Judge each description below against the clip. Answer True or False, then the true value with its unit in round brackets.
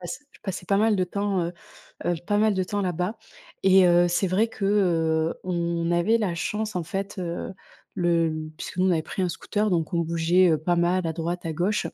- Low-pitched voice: False (180 Hz)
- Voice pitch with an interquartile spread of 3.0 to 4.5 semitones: False (2.6 semitones)